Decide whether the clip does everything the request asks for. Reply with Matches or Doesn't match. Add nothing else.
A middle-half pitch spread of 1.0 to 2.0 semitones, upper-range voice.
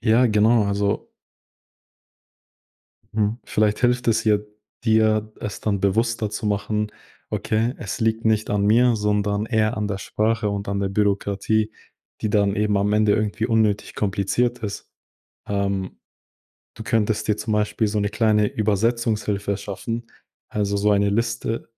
Doesn't match